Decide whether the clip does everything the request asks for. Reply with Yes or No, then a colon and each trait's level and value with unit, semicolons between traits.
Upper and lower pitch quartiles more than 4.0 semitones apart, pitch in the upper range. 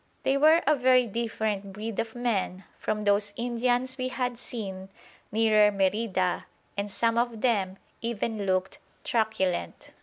No: average, 3.4 semitones; high, 220 Hz